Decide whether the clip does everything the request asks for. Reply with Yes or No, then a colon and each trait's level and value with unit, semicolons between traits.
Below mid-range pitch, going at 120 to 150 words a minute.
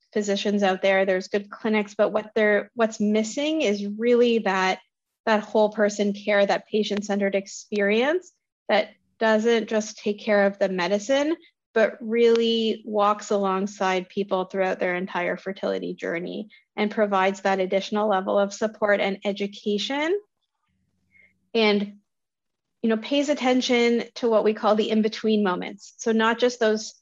No: high, 210 Hz; average, 145 wpm